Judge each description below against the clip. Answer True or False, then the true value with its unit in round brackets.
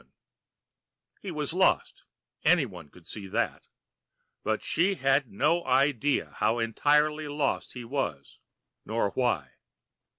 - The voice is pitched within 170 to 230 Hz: False (135 Hz)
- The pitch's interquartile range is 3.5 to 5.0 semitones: False (5.4 semitones)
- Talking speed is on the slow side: True (120 wpm)